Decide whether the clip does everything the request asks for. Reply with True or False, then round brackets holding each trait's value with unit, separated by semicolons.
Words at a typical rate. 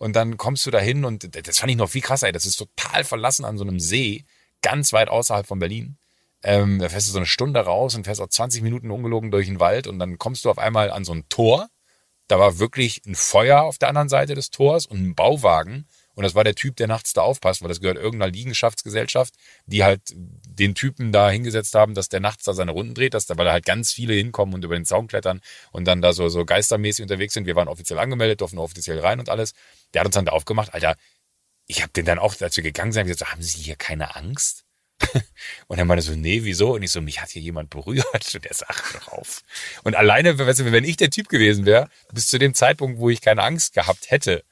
False (250 wpm)